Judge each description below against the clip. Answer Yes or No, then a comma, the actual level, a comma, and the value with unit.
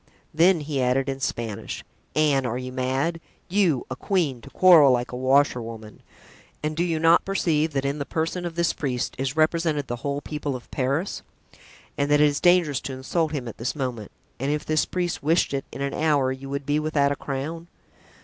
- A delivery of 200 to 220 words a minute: Yes, fast, 205 wpm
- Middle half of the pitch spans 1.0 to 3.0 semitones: No, average, 3.4 semitones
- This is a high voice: No, medium, 145 Hz